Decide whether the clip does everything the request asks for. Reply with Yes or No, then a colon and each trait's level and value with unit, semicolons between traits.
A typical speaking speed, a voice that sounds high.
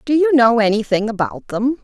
Yes: average, 195 wpm; high, 240 Hz